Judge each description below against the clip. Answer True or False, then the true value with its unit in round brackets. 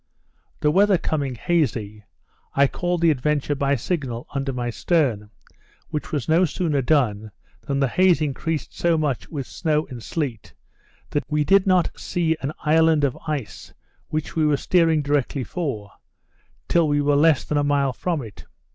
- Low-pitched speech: False (145 Hz)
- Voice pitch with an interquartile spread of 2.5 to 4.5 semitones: True (3.4 semitones)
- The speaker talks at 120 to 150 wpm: False (165 wpm)